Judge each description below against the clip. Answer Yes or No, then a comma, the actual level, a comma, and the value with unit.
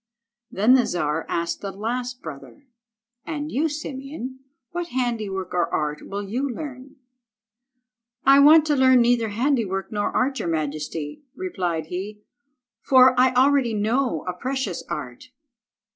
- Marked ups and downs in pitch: Yes, wide, 6.5 semitones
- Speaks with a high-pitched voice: Yes, high, 240 Hz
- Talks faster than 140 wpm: No, slow, 135 wpm